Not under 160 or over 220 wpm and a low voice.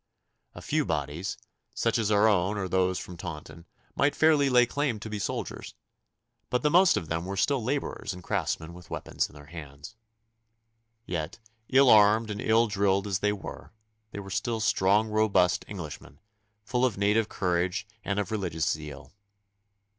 Yes: average, 170 wpm; low, 100 Hz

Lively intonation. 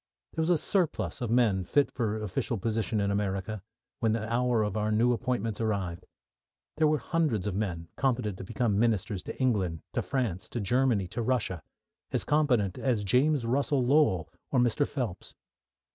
No: average, 4.2 semitones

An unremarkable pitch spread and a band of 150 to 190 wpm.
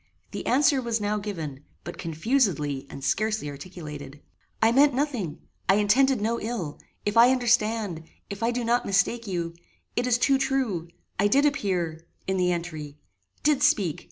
No: wide, 6.4 semitones; average, 160 wpm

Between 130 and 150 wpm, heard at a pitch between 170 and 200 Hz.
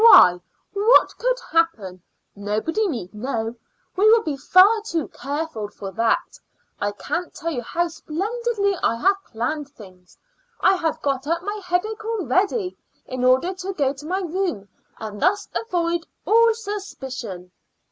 No: average, 145 wpm; very high, 330 Hz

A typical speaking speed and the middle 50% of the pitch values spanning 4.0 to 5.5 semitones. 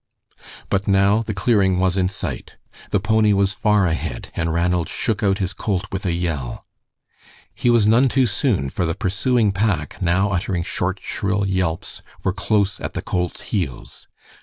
No: average, 170 wpm; average, 2.9 semitones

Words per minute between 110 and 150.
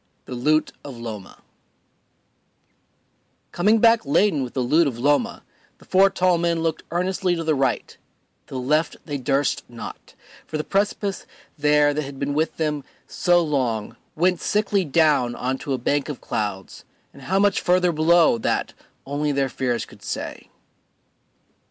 No: average, 160 wpm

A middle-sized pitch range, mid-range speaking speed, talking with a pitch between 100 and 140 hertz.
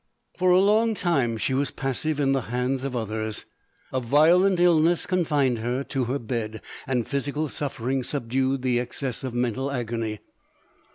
Yes: average, 3.7 semitones; average, 160 wpm; low, 135 Hz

